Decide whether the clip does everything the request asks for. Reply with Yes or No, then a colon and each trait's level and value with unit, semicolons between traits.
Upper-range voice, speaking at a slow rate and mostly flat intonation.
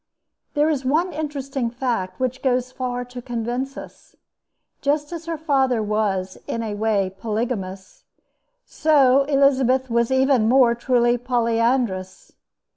No: very high, 250 Hz; slow, 125 wpm; average, 3.0 semitones